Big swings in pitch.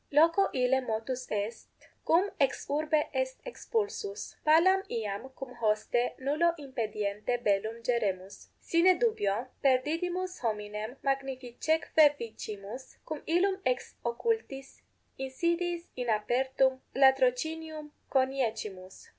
Yes: wide, 6.0 semitones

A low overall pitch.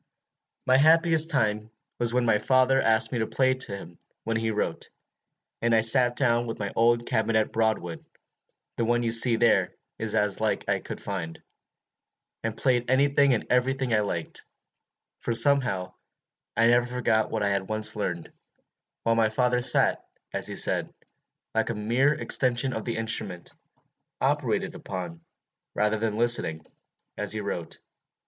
Yes: low, 115 Hz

